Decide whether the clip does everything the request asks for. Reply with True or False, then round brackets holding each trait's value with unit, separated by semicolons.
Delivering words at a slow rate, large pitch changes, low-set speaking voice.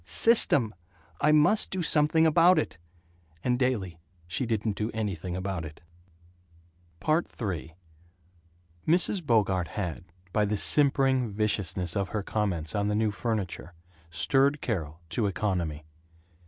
True (125 wpm; 6.8 semitones; 105 Hz)